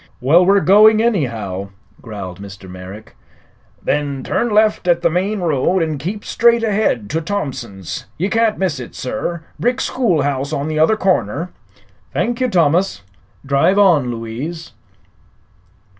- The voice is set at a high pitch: No, medium, 165 Hz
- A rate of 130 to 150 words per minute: Yes, average, 140 wpm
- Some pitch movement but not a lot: No, wide, 8.0 semitones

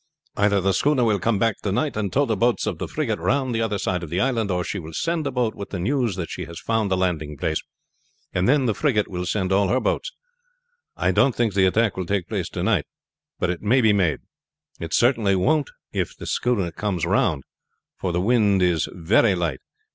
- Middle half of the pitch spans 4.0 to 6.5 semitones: Yes, average, 4.7 semitones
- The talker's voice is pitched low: Yes, low, 100 Hz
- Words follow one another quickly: Yes, fast, 230 wpm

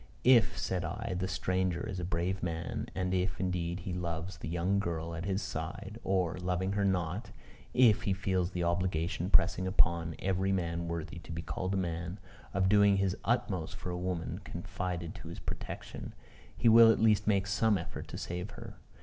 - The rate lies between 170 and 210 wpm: Yes, average, 190 wpm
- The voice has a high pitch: No, very low, 90 Hz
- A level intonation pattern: Yes, narrow, 2.2 semitones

